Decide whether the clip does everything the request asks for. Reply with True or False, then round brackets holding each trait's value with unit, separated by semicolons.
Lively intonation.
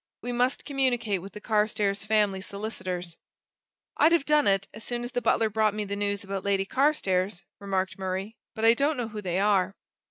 False (3.4 semitones)